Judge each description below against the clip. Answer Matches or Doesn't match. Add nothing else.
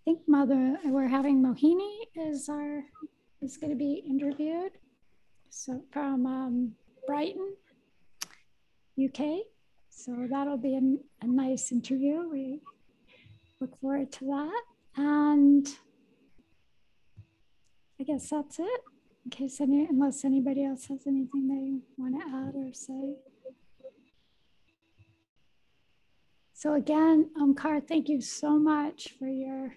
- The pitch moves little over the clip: Matches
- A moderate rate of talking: Doesn't match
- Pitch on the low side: Doesn't match